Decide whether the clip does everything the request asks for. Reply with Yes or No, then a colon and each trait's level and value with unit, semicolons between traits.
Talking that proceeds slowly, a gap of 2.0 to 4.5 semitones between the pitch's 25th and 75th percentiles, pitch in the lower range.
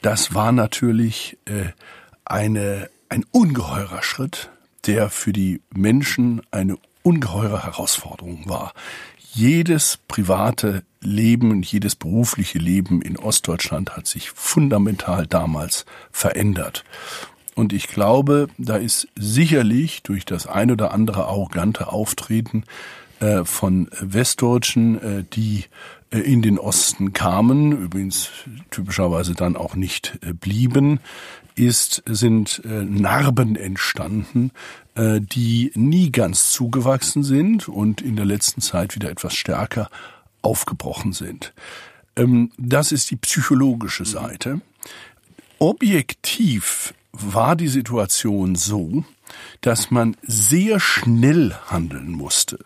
Yes: slow, 100 wpm; average, 4.1 semitones; low, 110 Hz